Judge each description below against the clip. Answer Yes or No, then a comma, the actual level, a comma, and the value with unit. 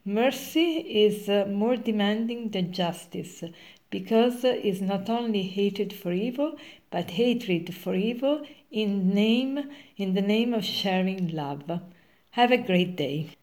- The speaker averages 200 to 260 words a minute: No, average, 140 wpm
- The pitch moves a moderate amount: Yes, average, 4.6 semitones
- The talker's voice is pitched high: Yes, high, 205 Hz